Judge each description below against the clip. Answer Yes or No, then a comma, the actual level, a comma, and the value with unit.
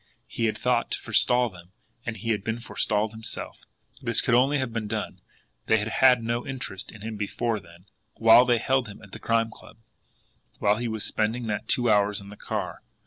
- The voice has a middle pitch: No, low, 110 Hz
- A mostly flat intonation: Yes, narrow, 2.3 semitones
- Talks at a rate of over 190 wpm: Yes, fast, 205 wpm